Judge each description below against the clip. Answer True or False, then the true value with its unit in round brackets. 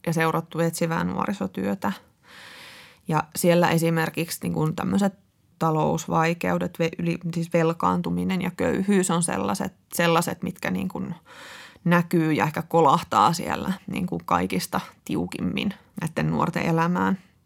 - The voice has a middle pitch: True (165 Hz)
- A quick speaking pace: False (115 wpm)